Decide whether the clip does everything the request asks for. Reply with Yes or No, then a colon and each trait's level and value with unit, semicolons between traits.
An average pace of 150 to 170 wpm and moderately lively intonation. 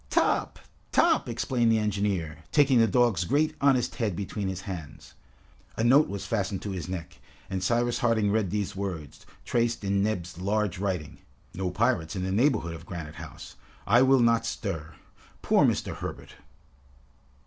Yes: average, 160 wpm; average, 4.2 semitones